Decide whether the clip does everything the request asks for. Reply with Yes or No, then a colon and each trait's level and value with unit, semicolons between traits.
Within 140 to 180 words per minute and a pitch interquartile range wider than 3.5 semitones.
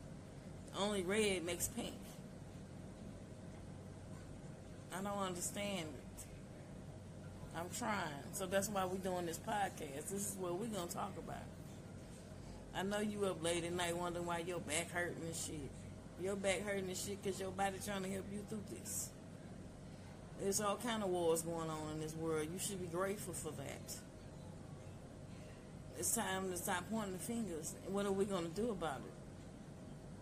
No: average, 165 wpm; average, 2.8 semitones